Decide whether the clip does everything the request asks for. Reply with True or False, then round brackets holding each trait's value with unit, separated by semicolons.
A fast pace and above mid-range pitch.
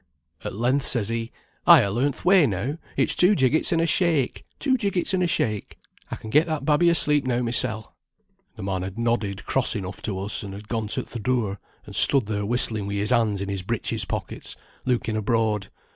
False (210 wpm; 115 Hz)